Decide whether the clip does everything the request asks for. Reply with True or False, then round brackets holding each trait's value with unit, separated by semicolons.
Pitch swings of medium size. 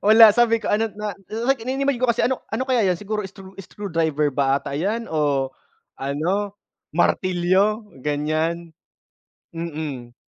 False (6.1 semitones)